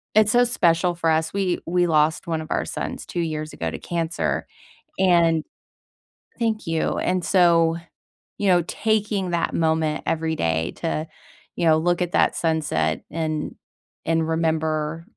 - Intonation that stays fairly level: Yes, narrow, 1.9 semitones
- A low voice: No, medium, 165 Hz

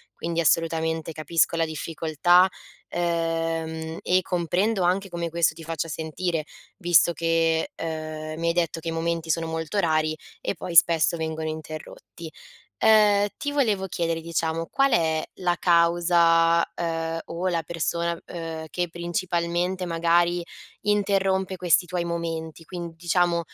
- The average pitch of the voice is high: No, medium, 170 Hz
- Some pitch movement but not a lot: No, narrow, 1.4 semitones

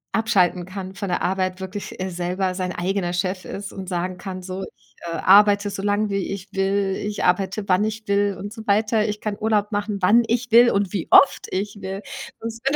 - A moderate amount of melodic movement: No, narrow, 2.0 semitones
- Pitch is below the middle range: No, high, 200 Hz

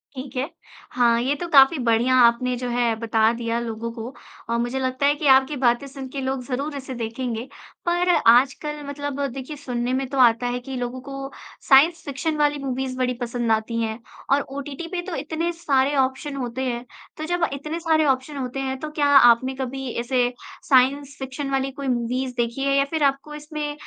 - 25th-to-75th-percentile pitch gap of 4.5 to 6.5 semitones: No, average, 2.8 semitones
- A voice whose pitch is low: No, very high, 265 Hz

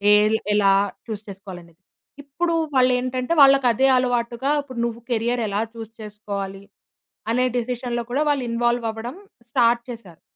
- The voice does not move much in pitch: No, average, 3.2 semitones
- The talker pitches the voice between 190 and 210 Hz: No, high, 235 Hz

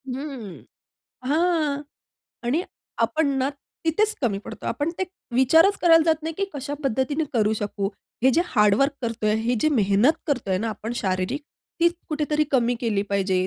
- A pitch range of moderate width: No, wide, 6.4 semitones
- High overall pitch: Yes, very high, 265 Hz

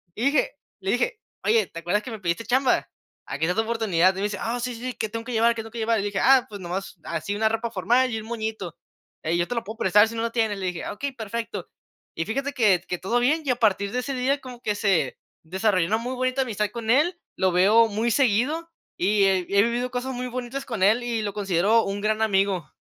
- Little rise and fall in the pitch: No, average, 3.7 semitones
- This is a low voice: No, high, 225 Hz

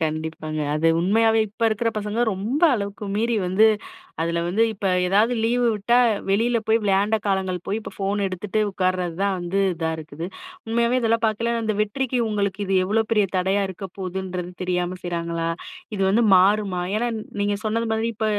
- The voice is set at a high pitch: Yes, high, 200 Hz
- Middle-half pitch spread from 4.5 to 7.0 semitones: No, average, 3.5 semitones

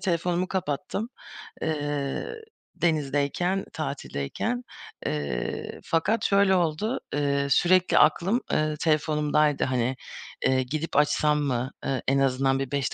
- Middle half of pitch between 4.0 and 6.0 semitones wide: Yes, average, 4.3 semitones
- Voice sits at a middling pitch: Yes, medium, 150 Hz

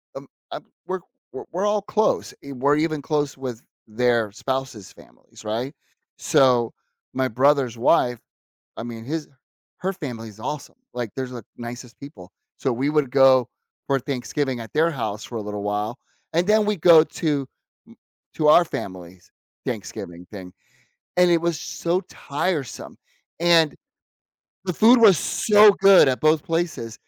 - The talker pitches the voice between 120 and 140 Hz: Yes, low, 135 Hz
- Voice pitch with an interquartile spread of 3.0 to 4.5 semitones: No, wide, 5.6 semitones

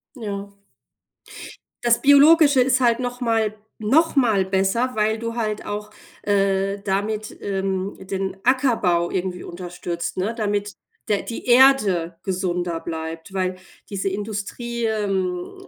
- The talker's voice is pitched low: No, high, 205 Hz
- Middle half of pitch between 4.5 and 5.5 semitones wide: No, average, 3.7 semitones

